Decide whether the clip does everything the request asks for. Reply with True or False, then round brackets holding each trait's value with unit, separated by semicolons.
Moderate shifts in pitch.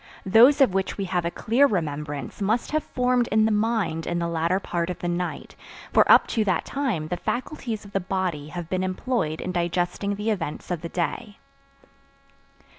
True (4.4 semitones)